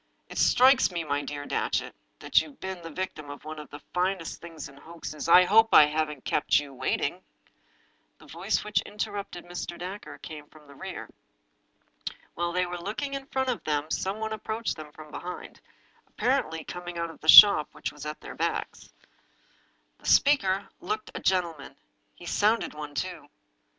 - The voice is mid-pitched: Yes, medium, 175 Hz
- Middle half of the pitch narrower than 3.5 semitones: No, average, 4.9 semitones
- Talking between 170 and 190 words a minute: Yes, average, 185 wpm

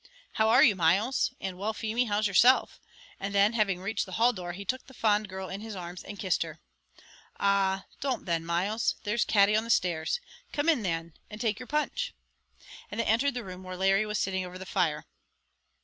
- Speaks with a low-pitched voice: No, high, 200 Hz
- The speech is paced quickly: Yes, fast, 210 wpm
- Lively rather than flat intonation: No, average, 3.3 semitones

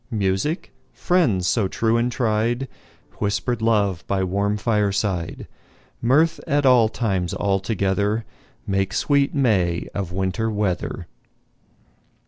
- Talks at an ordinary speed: No, slow, 100 wpm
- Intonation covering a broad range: No, average, 3.6 semitones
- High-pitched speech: No, low, 105 Hz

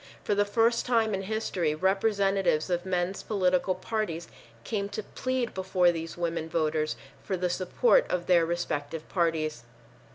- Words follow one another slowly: No, average, 150 wpm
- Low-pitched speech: No, medium, 185 Hz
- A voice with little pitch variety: No, average, 3.5 semitones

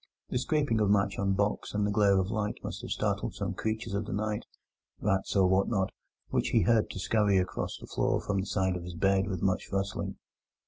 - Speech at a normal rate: No, fast, 210 wpm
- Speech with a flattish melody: Yes, narrow, 1.8 semitones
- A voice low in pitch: Yes, low, 100 Hz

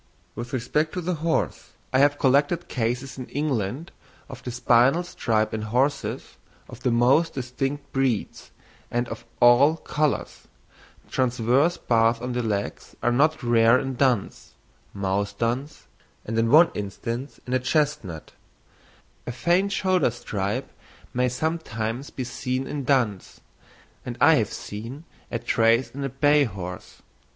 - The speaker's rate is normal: Yes, average, 145 wpm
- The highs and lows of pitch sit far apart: No, average, 3.8 semitones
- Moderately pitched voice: No, low, 125 Hz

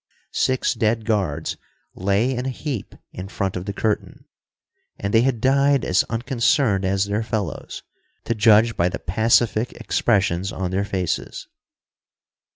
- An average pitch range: Yes, average, 3.5 semitones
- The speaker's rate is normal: Yes, average, 145 wpm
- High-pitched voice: No, low, 110 Hz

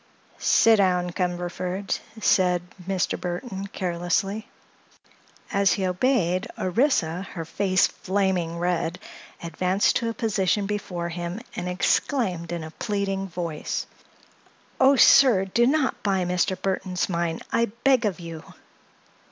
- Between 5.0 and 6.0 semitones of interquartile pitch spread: No, narrow, 2.6 semitones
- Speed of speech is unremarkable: No, slow, 120 wpm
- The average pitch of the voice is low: No, medium, 185 Hz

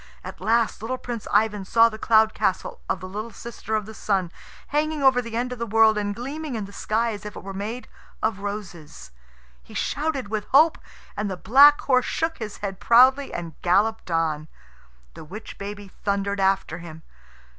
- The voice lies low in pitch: No, high, 215 Hz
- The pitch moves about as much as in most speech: Yes, average, 3.3 semitones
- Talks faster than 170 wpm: Yes, average, 190 wpm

